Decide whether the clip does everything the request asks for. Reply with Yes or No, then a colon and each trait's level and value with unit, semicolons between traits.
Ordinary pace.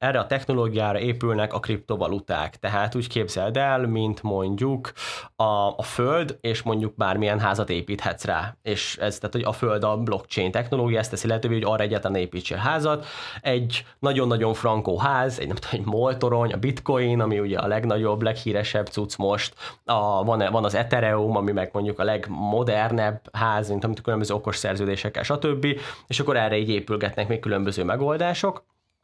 No: fast, 165 wpm